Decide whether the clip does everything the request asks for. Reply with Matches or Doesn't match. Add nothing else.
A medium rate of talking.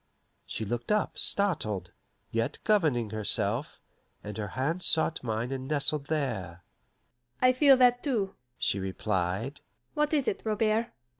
Doesn't match